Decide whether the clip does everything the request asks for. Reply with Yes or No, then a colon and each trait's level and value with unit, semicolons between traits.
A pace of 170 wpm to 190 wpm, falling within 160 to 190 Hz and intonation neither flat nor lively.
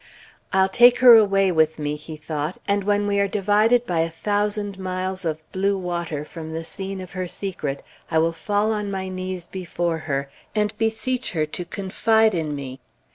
Yes: average, 185 wpm; medium, 185 Hz; average, 4.1 semitones